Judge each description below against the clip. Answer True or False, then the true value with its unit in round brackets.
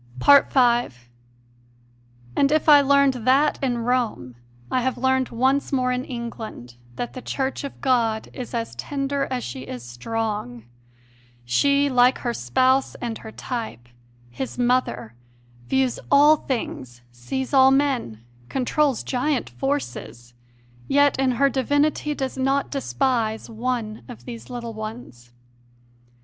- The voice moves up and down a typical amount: True (3.6 semitones)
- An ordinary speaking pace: False (130 wpm)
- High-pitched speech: True (250 Hz)